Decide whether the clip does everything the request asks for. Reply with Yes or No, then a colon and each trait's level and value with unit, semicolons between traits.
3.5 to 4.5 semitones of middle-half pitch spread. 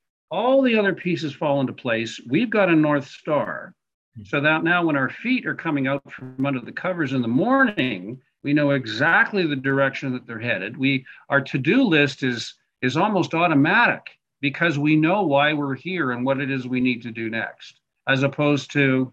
Yes: average, 4.0 semitones